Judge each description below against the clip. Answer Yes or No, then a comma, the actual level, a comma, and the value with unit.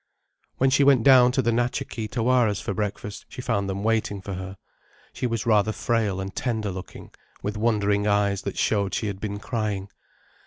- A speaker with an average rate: Yes, average, 190 wpm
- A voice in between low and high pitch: No, low, 105 Hz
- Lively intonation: No, average, 2.8 semitones